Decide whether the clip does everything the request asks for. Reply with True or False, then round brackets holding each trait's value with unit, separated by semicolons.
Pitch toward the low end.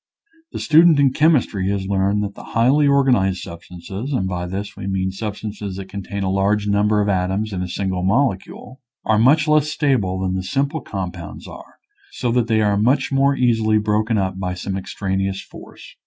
True (100 Hz)